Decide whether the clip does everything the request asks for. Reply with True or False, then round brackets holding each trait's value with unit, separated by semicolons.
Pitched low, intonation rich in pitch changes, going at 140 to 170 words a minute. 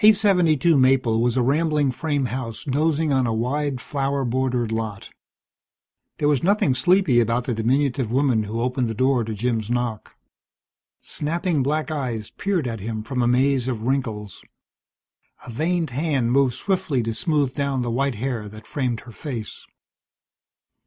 False (130 Hz; 3.9 semitones; 160 wpm)